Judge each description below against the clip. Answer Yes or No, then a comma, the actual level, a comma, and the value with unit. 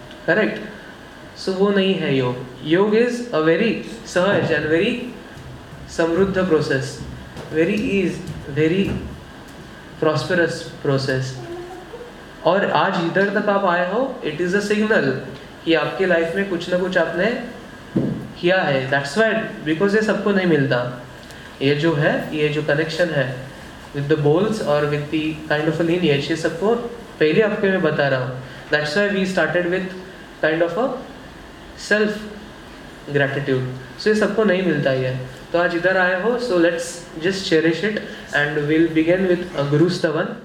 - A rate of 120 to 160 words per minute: Yes, average, 155 wpm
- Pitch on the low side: No, medium, 170 Hz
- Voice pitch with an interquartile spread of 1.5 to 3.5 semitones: No, average, 4.6 semitones